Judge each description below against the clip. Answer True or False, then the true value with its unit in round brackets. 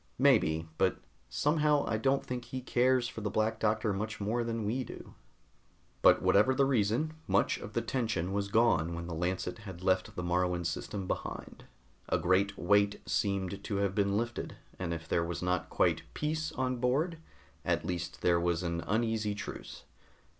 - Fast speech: False (175 wpm)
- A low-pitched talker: True (105 Hz)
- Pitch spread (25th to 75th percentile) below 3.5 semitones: False (5.0 semitones)